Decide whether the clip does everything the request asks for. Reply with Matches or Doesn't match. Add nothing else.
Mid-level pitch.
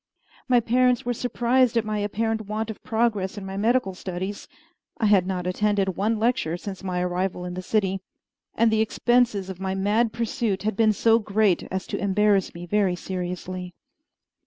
Doesn't match